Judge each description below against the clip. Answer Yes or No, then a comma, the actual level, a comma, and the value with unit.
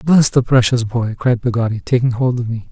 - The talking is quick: Yes, fast, 220 wpm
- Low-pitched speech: Yes, low, 120 Hz